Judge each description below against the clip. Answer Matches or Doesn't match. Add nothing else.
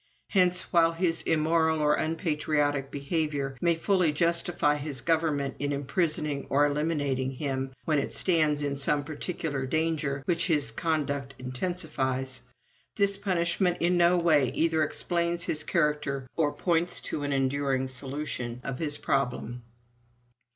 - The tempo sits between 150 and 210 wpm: Doesn't match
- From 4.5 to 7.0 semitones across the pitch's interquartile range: Doesn't match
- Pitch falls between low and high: Matches